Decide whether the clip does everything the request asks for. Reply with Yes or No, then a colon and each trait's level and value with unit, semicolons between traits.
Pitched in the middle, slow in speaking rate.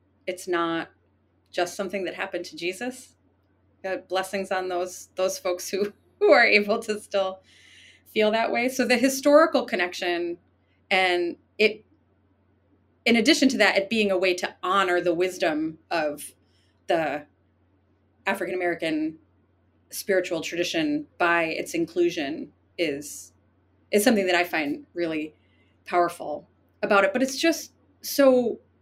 Yes: medium, 175 Hz; slow, 130 wpm